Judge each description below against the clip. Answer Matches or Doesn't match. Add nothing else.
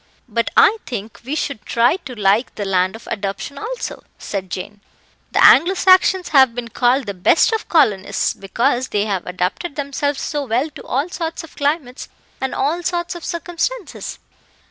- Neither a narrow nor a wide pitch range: Doesn't match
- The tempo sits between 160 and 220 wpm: Matches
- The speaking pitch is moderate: Doesn't match